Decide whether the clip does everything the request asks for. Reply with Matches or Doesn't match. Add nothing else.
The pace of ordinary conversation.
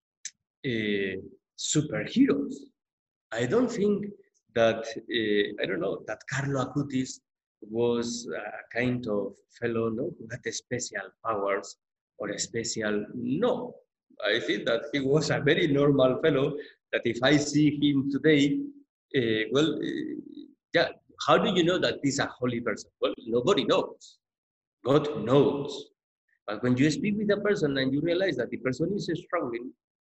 Matches